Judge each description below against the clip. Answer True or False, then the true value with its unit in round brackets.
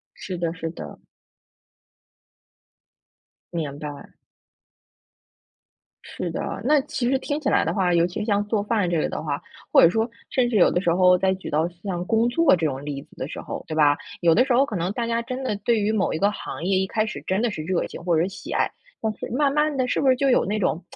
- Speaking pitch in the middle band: False (195 Hz)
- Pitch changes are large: True (5.8 semitones)